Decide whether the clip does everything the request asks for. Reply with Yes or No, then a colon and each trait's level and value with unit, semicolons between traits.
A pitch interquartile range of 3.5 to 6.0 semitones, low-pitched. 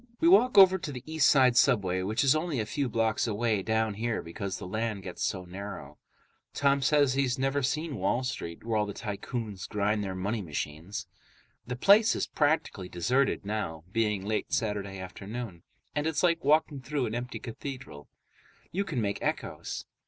Yes: wide, 5.6 semitones; low, 115 Hz